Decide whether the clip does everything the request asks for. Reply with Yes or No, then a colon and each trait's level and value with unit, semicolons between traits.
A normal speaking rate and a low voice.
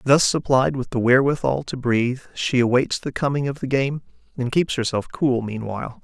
Yes: average, 190 wpm; low, 130 Hz